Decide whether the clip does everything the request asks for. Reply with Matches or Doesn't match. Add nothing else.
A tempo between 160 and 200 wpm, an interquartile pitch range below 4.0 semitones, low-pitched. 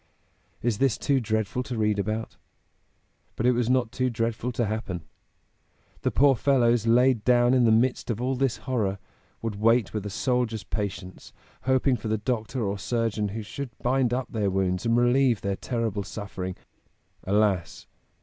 Matches